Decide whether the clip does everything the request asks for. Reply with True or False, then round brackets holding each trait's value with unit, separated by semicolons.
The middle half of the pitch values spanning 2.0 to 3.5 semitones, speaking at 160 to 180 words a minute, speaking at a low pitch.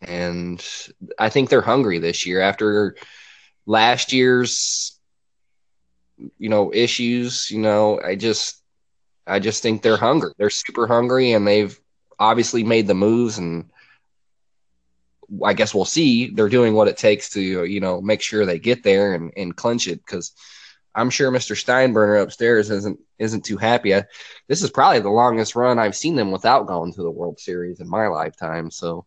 False (4.3 semitones; 170 wpm; 105 Hz)